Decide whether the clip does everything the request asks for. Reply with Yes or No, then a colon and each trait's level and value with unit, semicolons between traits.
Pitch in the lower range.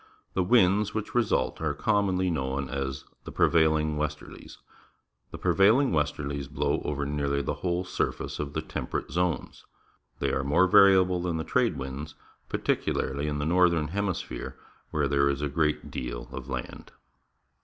Yes: very low, 75 Hz